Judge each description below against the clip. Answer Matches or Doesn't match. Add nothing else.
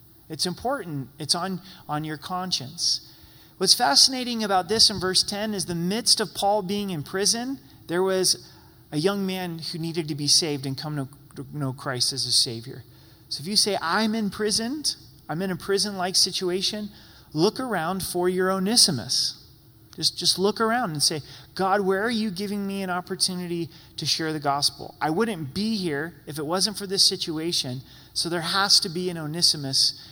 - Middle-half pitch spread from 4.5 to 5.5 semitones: Matches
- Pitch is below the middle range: Doesn't match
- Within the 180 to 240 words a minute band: Matches